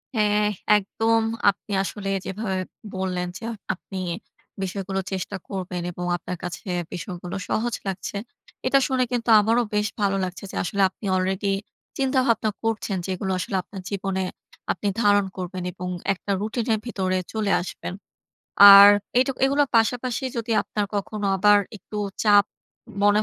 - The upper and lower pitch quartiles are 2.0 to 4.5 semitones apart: Yes, average, 2.9 semitones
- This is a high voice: Yes, high, 205 Hz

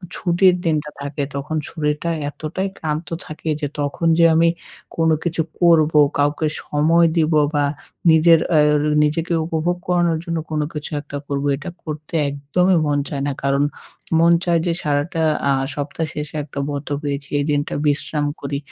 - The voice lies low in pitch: No, medium, 155 Hz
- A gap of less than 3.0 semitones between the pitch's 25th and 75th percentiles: Yes, narrow, 2.4 semitones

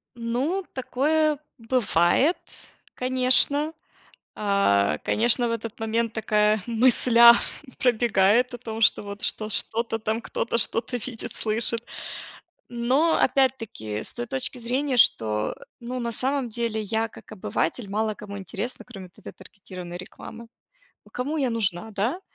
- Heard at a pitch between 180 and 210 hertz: No, high, 230 Hz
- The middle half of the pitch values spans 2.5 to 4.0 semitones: Yes, average, 3.1 semitones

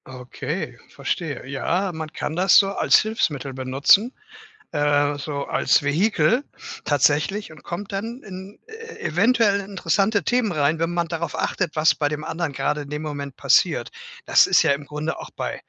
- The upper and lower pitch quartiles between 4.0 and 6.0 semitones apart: Yes, wide, 5.5 semitones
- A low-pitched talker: No, medium, 160 Hz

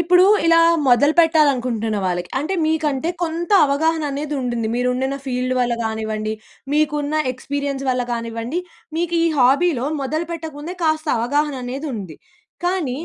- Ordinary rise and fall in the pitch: Yes, average, 4.3 semitones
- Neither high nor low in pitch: No, very high, 280 Hz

